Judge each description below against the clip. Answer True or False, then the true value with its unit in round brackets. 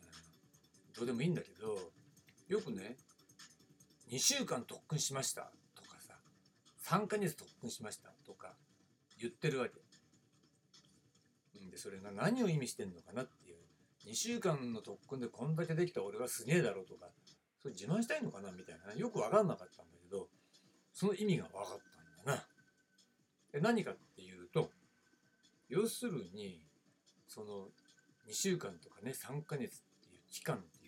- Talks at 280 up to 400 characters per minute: True (290 characters per minute)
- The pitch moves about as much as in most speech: False (7.6 semitones)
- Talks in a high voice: False (165 Hz)